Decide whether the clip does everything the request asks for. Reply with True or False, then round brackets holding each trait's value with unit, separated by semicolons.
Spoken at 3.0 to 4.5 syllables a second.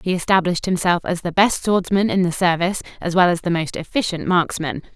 False (5.9 syllables/s)